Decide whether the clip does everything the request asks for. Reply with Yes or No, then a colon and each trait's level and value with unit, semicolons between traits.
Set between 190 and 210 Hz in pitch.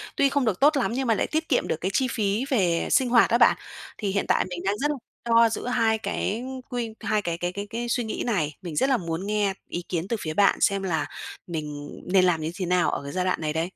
Yes: high, 200 Hz